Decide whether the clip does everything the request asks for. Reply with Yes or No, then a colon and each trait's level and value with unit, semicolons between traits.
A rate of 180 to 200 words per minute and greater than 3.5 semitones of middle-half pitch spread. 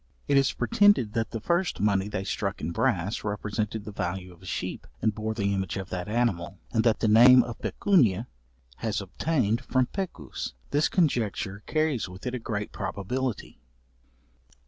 No: average, 170 wpm; average, 4.3 semitones